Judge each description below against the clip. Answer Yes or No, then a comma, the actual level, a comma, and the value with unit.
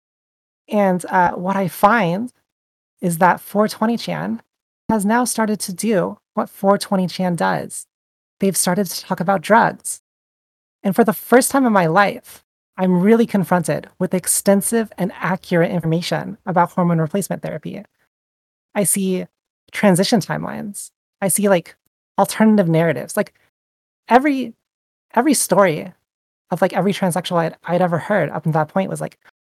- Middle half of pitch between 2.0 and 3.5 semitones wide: Yes, average, 3.1 semitones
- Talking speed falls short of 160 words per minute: Yes, average, 145 wpm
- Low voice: No, high, 190 Hz